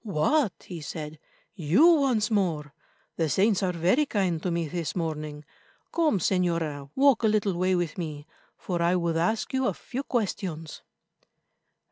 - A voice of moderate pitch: Yes, medium, 180 Hz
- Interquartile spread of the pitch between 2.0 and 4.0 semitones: No, average, 5.1 semitones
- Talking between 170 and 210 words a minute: No, average, 155 wpm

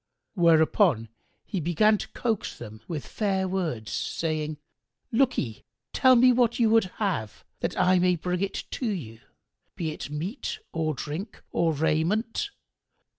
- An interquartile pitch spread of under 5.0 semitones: No, wide, 5.6 semitones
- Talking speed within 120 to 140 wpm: Yes, slow, 135 wpm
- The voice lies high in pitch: No, medium, 180 Hz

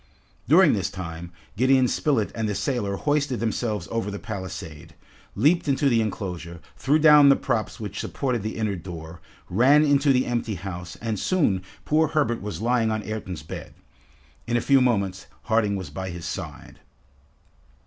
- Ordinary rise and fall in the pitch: No, wide, 5.8 semitones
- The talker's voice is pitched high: No, low, 110 Hz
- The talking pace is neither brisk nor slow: Yes, average, 165 wpm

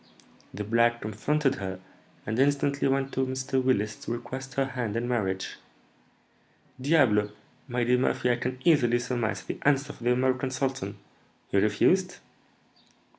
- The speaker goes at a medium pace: Yes, average, 145 wpm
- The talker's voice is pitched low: Yes, low, 125 Hz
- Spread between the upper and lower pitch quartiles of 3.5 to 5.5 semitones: No, average, 2.8 semitones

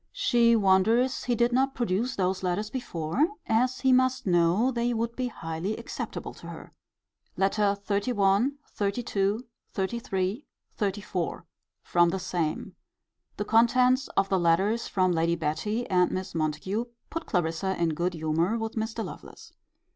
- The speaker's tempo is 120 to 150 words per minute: Yes, average, 140 wpm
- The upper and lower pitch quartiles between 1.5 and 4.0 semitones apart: No, average, 4.7 semitones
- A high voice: Yes, high, 200 Hz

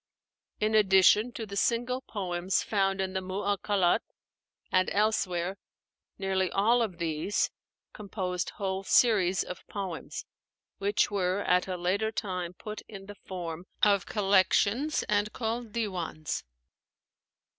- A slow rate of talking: Yes, slow, 125 wpm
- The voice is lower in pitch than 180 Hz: No, high, 195 Hz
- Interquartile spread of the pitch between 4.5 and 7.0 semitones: No, narrow, 2.4 semitones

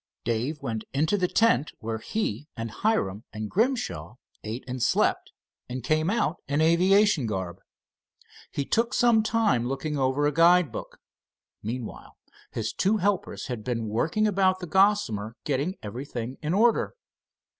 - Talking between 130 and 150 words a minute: Yes, average, 145 wpm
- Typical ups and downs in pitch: No, wide, 8.9 semitones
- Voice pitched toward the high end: No, medium, 145 Hz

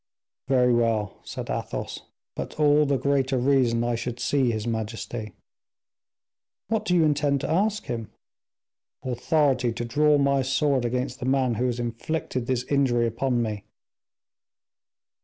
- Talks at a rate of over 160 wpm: No, average, 140 wpm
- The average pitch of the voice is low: Yes, low, 130 Hz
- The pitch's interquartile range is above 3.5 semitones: No, average, 3.0 semitones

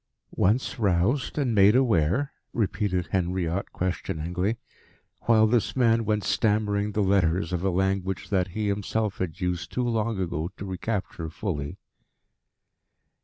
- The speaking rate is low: Yes, slow, 130 wpm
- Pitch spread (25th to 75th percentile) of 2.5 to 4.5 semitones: Yes, average, 3.4 semitones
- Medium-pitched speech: No, low, 100 Hz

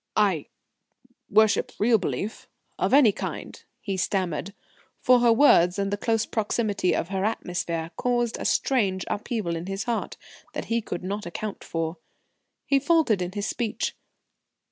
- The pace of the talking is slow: No, average, 150 wpm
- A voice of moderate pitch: No, high, 205 Hz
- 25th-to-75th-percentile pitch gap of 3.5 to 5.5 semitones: Yes, average, 3.9 semitones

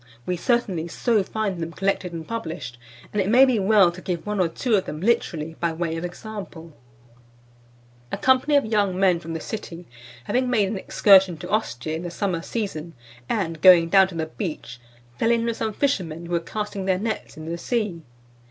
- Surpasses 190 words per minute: Yes, average, 200 wpm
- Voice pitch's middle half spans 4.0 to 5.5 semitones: Yes, average, 4.6 semitones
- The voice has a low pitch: No, medium, 185 Hz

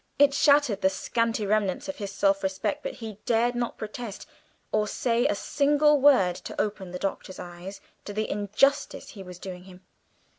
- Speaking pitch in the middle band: No, high, 210 Hz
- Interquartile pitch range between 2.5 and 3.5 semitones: No, average, 4.1 semitones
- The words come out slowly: No, average, 180 wpm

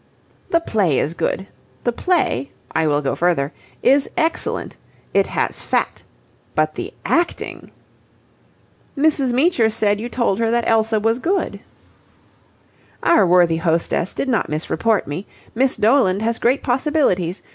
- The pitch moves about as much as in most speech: No, wide, 6.9 semitones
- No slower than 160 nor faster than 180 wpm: No, slow, 135 wpm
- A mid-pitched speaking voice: No, high, 225 Hz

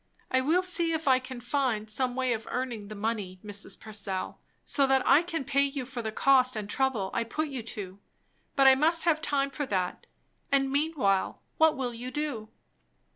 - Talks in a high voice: Yes, very high, 260 Hz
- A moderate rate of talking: Yes, average, 195 wpm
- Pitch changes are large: No, average, 4.7 semitones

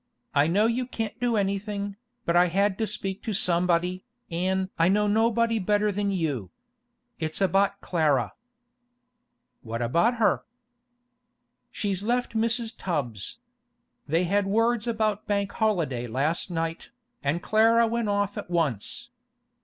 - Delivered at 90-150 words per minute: Yes, slow, 135 wpm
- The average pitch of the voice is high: Yes, high, 200 Hz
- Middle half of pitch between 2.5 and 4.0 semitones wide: No, average, 4.5 semitones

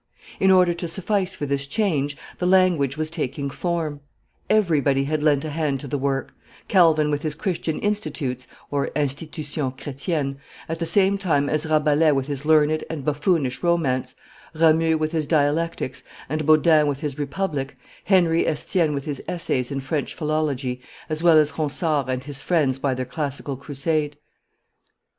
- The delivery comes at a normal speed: Yes, average, 160 wpm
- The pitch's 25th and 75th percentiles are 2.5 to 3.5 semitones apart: Yes, average, 2.8 semitones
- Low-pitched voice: No, medium, 150 Hz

